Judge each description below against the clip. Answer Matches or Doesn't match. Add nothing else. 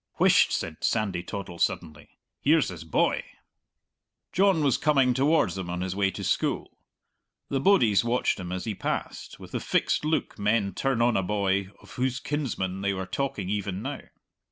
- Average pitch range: Doesn't match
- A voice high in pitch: Doesn't match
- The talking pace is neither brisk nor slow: Matches